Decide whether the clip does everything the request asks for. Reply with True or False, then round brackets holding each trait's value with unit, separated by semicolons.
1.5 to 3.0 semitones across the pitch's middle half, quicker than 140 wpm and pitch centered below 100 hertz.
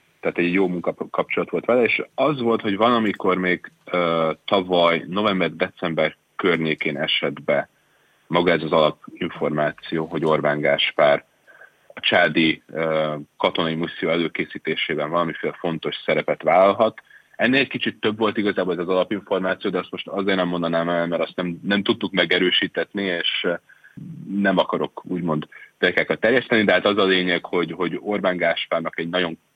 True (2.6 semitones; 150 wpm; 85 Hz)